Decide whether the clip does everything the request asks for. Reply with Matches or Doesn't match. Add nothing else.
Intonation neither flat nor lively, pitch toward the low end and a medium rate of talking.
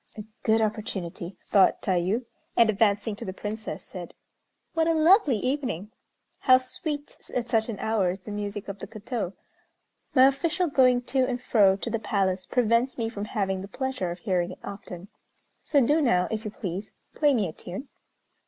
Doesn't match